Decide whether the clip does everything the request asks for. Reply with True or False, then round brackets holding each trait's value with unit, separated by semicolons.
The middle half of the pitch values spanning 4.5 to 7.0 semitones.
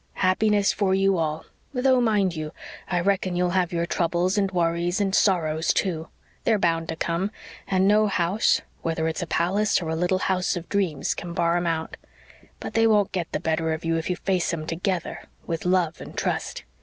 False (2.9 semitones)